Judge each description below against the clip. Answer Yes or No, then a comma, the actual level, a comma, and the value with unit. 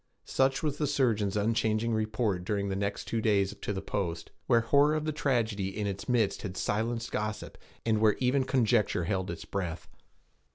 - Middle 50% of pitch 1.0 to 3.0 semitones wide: No, average, 3.4 semitones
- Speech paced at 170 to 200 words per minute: Yes, average, 180 wpm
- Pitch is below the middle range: Yes, low, 110 Hz